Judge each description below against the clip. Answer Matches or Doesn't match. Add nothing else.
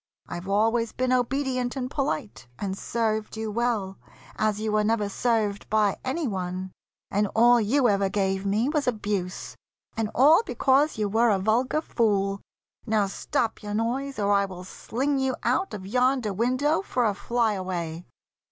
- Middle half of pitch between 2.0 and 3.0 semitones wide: Doesn't match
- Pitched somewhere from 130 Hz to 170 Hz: Doesn't match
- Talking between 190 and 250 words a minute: Doesn't match